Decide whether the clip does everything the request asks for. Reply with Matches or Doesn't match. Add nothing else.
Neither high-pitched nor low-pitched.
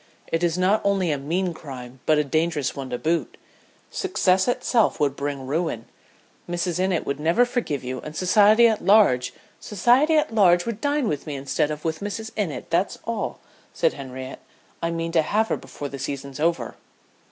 Matches